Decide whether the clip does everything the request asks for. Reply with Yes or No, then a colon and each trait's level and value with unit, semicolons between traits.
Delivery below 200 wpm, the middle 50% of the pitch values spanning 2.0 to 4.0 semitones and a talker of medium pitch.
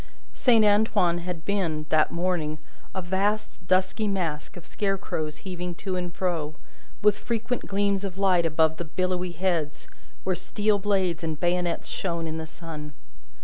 Yes: average, 150 wpm; average, 3.1 semitones; medium, 180 Hz